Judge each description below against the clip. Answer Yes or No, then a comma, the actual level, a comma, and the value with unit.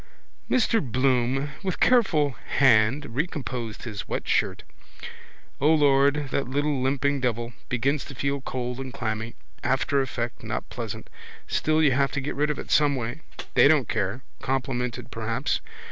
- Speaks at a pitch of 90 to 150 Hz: Yes, low, 135 Hz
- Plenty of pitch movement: No, average, 2.8 semitones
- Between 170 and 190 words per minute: No, average, 145 wpm